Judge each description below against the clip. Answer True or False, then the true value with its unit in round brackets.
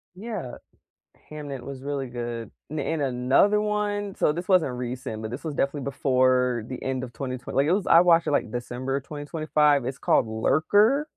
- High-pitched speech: False (140 Hz)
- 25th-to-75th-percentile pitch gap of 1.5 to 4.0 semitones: False (4.7 semitones)